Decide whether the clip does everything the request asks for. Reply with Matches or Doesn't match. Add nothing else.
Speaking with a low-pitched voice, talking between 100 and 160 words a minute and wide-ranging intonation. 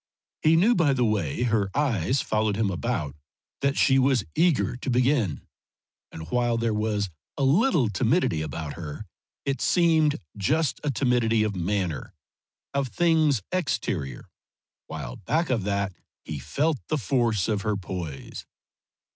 Matches